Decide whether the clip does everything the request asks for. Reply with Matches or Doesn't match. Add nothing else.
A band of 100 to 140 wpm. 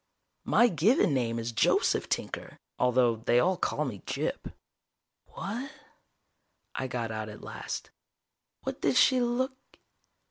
Matches